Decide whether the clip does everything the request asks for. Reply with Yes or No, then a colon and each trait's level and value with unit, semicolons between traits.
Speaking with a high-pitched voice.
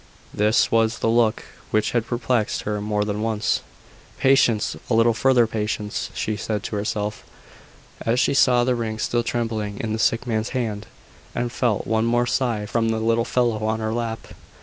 No: low, 115 Hz